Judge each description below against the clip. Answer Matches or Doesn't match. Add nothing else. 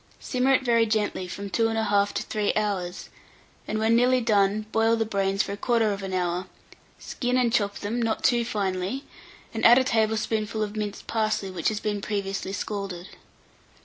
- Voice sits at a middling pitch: Doesn't match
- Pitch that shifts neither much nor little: Doesn't match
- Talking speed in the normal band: Matches